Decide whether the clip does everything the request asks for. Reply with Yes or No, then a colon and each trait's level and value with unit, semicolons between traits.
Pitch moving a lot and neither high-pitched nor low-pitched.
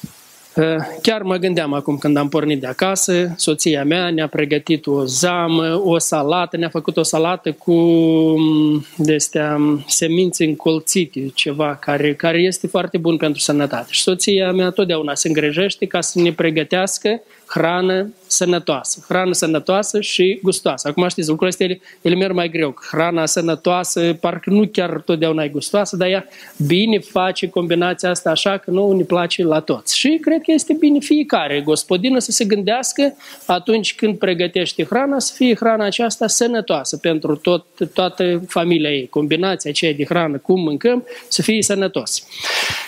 No: average, 3.3 semitones; medium, 175 Hz